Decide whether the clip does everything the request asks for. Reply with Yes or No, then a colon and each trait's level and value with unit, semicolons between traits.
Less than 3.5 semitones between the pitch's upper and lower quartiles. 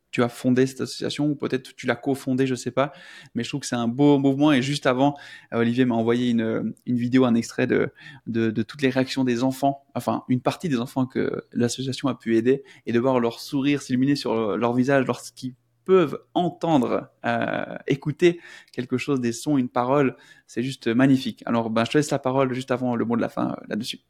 Yes: narrow, 2.6 semitones